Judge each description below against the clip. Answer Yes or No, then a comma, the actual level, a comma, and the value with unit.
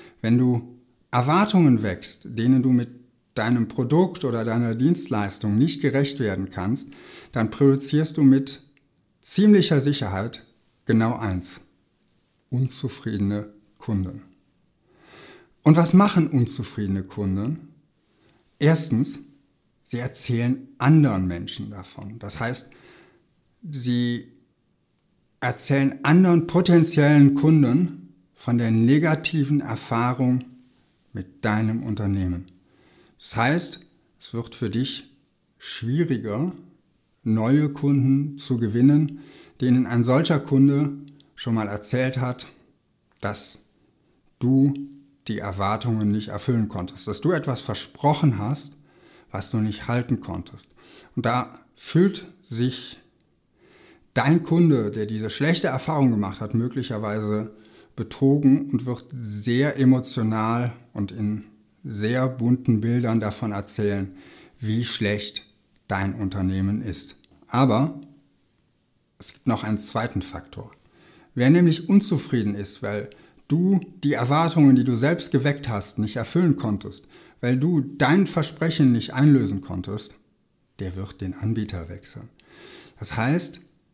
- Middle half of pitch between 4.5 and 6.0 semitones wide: Yes, average, 5.1 semitones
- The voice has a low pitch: Yes, low, 125 Hz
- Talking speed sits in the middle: No, slow, 110 wpm